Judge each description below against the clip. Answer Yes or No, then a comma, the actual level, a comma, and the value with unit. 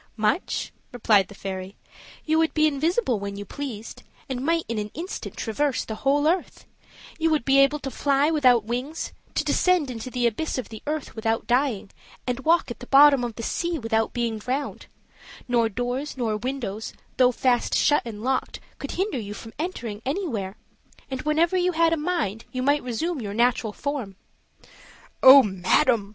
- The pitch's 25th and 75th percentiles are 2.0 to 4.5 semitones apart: No, average, 5.1 semitones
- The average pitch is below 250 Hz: No, very high, 255 Hz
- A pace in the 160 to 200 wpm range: Yes, average, 180 wpm